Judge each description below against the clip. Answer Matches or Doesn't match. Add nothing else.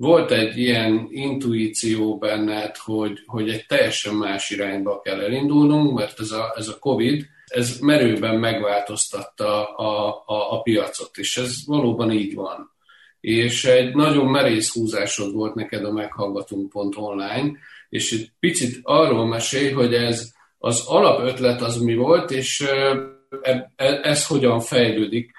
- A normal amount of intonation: Matches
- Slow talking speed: Doesn't match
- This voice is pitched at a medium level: Doesn't match